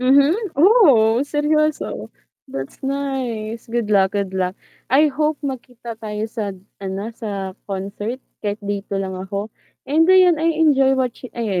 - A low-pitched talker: No, high, 235 Hz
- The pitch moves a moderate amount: No, wide, 5.7 semitones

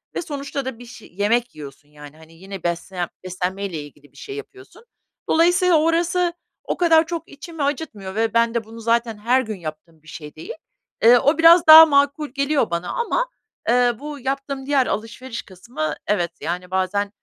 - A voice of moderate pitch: No, high, 235 Hz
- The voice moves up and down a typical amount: No, wide, 8.3 semitones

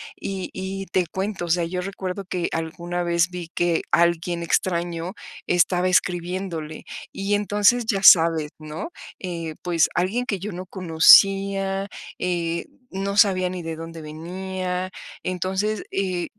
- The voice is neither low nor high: Yes, medium, 180 Hz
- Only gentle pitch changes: Yes, narrow, 2.2 semitones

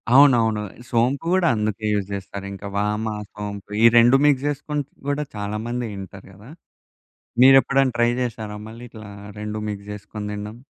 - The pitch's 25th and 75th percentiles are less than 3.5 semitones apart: No, average, 3.8 semitones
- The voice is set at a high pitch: No, low, 110 Hz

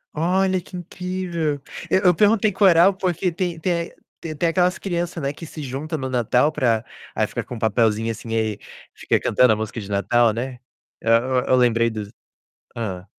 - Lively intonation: Yes, wide, 7.4 semitones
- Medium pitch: Yes, medium, 145 Hz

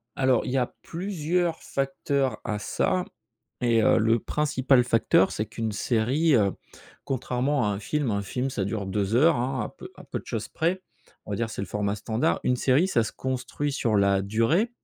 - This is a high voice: No, low, 125 Hz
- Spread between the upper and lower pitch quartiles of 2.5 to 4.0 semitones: No, average, 4.8 semitones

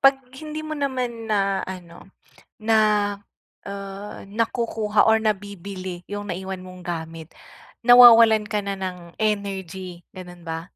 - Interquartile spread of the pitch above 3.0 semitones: Yes, average, 3.5 semitones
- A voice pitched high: Yes, high, 200 Hz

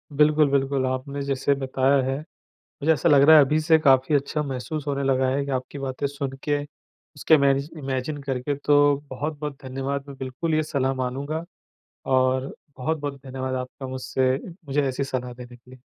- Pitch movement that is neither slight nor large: No, narrow, 1.8 semitones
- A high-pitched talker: No, medium, 140 Hz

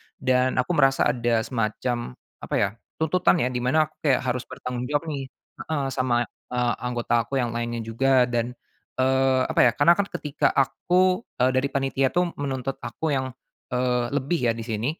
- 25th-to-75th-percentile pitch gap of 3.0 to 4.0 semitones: No, narrow, 2.5 semitones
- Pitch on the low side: Yes, low, 130 Hz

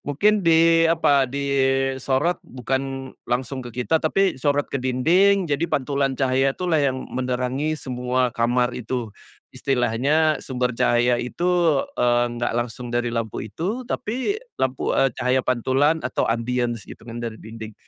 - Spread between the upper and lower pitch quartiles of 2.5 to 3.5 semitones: No, average, 3.9 semitones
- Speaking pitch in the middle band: No, low, 130 Hz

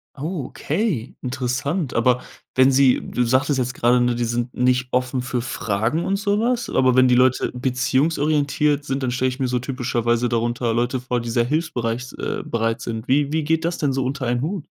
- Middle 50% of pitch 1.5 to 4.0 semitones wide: Yes, average, 2.9 semitones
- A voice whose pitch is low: Yes, low, 130 Hz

